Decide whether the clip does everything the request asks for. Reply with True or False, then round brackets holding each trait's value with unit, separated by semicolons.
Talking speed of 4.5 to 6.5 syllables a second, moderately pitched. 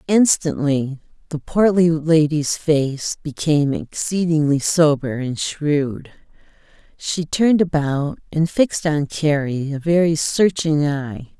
False (3.7 syllables/s; 155 Hz)